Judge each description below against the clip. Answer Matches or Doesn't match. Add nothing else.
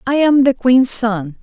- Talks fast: Doesn't match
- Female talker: Matches